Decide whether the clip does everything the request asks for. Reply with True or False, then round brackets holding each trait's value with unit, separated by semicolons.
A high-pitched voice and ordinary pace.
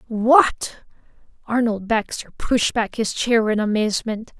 False (225 Hz; 125 wpm)